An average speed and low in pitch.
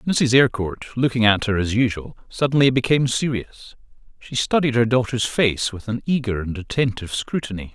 Yes: average, 165 wpm; low, 120 Hz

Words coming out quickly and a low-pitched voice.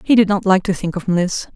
No: fast, 310 wpm; high, 190 Hz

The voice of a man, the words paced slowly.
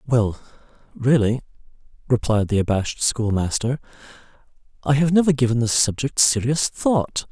Yes: male; slow, 115 wpm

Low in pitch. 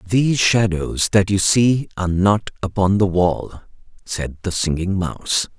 Yes: very low, 95 Hz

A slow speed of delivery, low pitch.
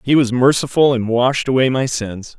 No: average, 200 wpm; low, 125 Hz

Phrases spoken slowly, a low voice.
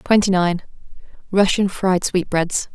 No: slow, 85 wpm; medium, 185 Hz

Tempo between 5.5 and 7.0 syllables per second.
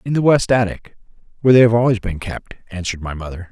Yes: 6.6 syllables/s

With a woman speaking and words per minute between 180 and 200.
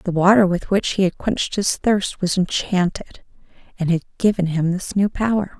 Yes: female; average, 195 wpm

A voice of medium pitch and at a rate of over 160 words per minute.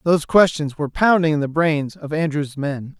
Yes: medium, 155 Hz; average, 200 wpm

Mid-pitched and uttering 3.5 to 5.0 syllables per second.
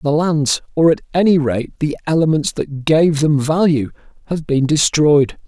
Yes: medium, 150 Hz; 4.4 syllables/s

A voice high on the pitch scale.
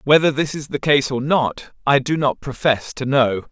No: medium, 140 Hz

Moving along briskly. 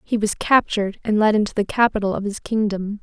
Yes: fast, 220 wpm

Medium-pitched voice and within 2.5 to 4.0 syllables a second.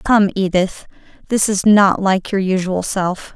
No: high, 195 Hz; 3.9 syllables/s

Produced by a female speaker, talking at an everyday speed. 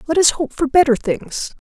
No: female; fast, 220 wpm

